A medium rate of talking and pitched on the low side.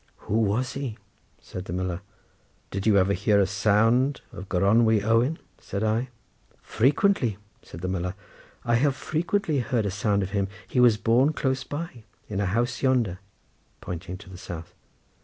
Yes: average, 165 wpm; low, 110 Hz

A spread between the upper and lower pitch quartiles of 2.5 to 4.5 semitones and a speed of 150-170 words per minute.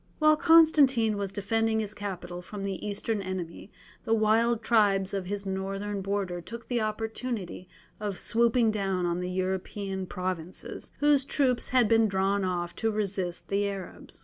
Yes: average, 3.0 semitones; average, 155 wpm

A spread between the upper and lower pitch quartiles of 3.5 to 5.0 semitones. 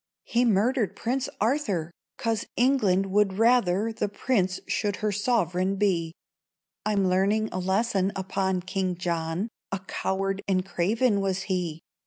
No: average, 2.9 semitones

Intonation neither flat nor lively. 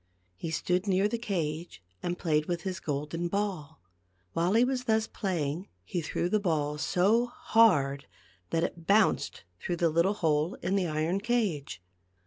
Yes: average, 4.6 semitones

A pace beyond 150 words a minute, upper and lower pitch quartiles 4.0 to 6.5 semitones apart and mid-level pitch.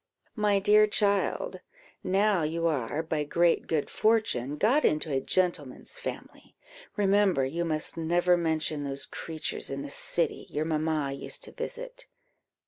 No: average, 140 wpm; average, 5.1 semitones; medium, 165 Hz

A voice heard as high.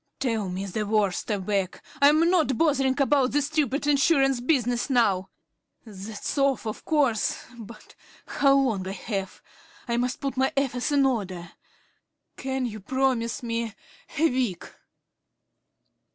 Yes: high, 245 Hz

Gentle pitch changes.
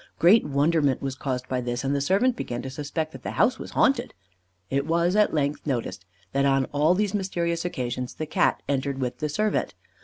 No: average, 4.3 semitones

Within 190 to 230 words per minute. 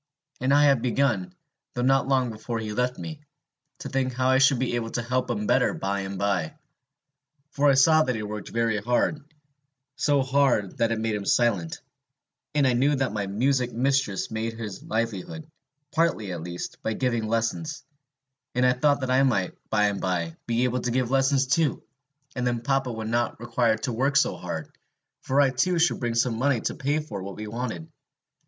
Yes: average, 200 wpm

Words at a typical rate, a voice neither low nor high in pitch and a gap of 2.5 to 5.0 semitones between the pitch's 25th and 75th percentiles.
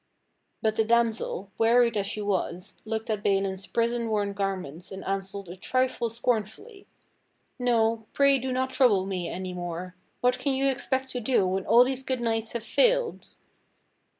No: average, 165 wpm; high, 225 Hz; average, 4.3 semitones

